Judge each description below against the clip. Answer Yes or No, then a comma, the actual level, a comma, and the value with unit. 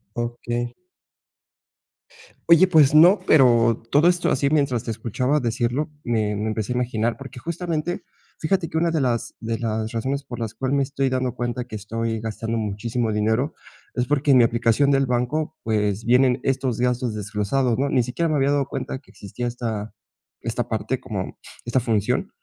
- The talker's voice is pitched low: Yes, low, 125 Hz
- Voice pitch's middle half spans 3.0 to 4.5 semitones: Yes, average, 3.5 semitones